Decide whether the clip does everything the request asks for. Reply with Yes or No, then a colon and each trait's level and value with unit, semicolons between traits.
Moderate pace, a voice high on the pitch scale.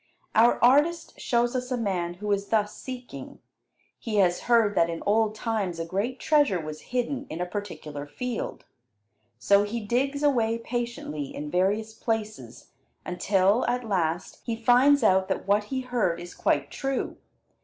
Yes: average, 160 wpm; high, 220 Hz